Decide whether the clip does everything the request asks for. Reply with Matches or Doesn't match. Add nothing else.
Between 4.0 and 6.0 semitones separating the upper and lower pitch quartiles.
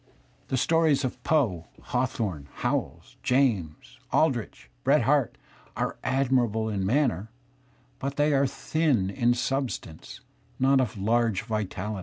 Matches